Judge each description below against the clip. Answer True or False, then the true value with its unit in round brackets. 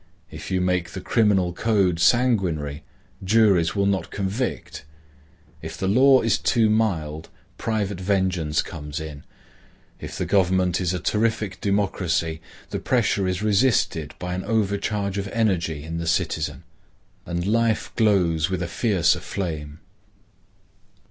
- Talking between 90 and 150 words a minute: True (135 wpm)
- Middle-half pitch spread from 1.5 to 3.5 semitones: False (4.0 semitones)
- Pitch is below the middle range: True (95 Hz)